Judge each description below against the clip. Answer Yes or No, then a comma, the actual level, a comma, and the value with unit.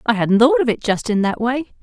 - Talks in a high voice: Yes, high, 240 Hz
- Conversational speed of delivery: No, fast, 295 wpm